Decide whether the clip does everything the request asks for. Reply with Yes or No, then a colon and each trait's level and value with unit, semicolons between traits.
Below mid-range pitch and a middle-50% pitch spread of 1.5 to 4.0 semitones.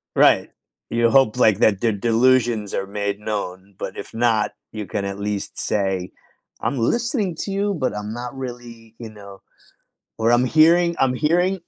No: low, 115 Hz; average, 4.4 semitones